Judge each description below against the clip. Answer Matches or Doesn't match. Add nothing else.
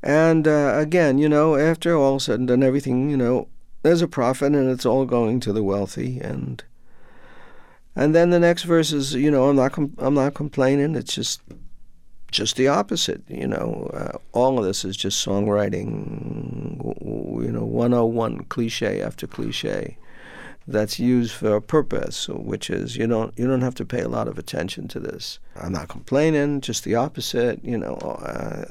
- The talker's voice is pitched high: Doesn't match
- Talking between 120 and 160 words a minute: Doesn't match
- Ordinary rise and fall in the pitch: Matches